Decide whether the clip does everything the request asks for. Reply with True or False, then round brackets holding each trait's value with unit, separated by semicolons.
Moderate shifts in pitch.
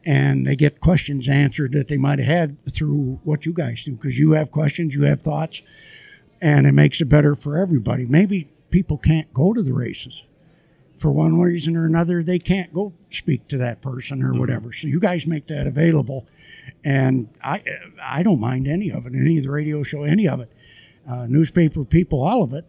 True (3.4 semitones)